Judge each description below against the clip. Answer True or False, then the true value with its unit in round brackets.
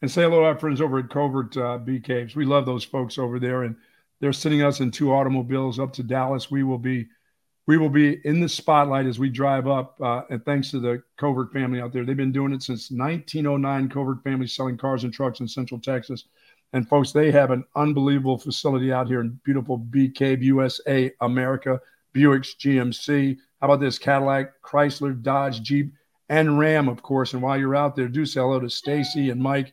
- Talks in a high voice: False (135 Hz)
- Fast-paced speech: True (210 wpm)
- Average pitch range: False (1.7 semitones)